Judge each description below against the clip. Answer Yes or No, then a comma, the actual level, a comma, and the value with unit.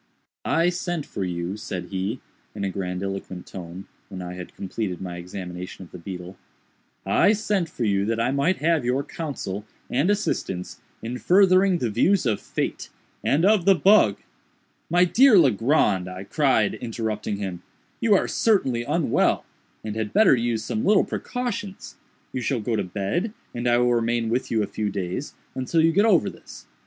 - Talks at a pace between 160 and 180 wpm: Yes, average, 175 wpm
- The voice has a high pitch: No, low, 115 Hz